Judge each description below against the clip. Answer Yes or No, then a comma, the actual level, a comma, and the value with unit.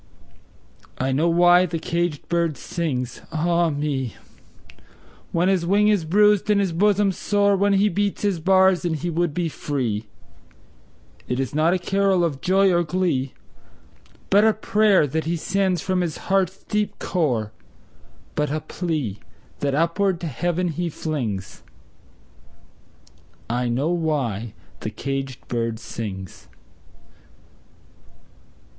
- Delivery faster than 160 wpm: No, slow, 135 wpm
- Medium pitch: Yes, medium, 170 Hz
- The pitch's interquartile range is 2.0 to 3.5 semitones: No, average, 5.2 semitones